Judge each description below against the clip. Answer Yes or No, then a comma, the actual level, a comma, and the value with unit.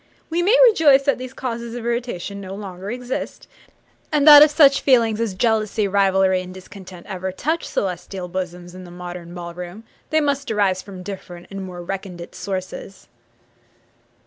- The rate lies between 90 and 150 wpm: No, average, 165 wpm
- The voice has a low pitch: No, high, 195 Hz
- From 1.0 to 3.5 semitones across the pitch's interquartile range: No, average, 5.2 semitones